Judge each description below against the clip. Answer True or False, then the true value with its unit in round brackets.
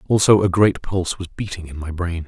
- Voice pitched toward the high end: False (90 Hz)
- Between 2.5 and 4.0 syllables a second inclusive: False (5.7 syllables/s)